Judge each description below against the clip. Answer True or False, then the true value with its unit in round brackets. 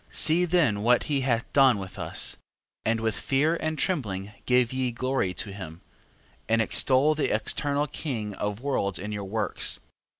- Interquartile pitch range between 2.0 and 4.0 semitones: False (5.4 semitones)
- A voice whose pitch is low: True (120 Hz)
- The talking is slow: False (170 wpm)